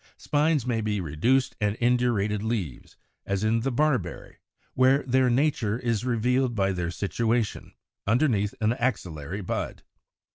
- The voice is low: Yes, low, 115 Hz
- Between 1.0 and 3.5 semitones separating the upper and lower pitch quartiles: No, average, 4.0 semitones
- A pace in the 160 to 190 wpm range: No, slow, 135 wpm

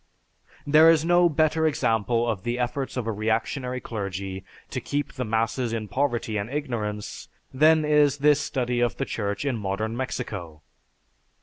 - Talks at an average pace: Yes, average, 160 wpm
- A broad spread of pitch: No, average, 5.0 semitones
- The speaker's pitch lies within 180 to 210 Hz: No, low, 120 Hz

